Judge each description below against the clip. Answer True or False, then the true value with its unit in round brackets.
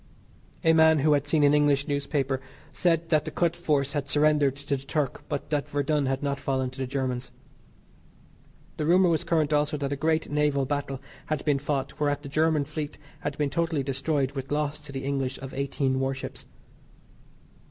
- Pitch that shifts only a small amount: True (1.9 semitones)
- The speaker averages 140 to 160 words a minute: False (190 wpm)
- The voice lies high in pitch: False (145 Hz)